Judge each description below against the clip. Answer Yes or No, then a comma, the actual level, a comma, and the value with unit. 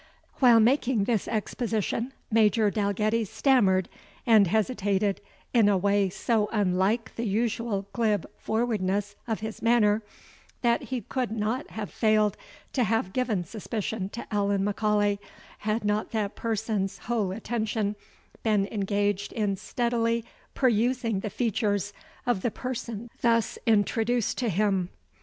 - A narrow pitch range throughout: Yes, narrow, 2.3 semitones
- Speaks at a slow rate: Yes, slow, 130 wpm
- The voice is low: No, high, 215 Hz